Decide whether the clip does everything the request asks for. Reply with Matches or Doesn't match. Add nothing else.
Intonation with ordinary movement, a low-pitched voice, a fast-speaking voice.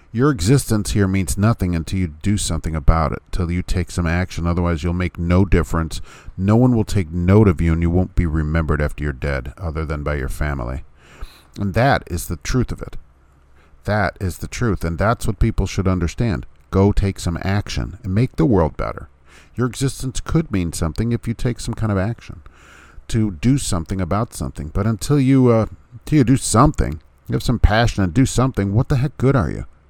Doesn't match